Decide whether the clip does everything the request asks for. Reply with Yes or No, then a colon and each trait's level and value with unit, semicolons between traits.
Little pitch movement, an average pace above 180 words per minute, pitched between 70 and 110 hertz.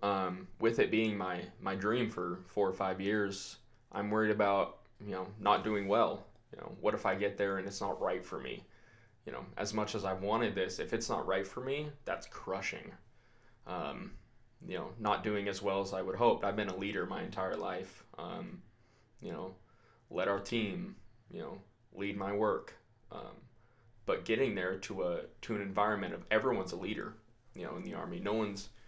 Yes: narrow, 2.3 semitones; fast, 205 wpm; low, 100 Hz